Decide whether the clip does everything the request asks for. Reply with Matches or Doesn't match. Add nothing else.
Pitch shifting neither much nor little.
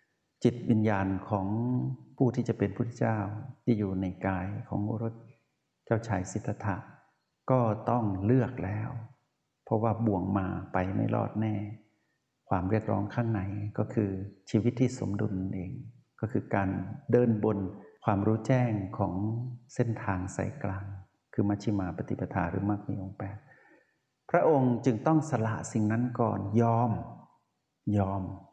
Matches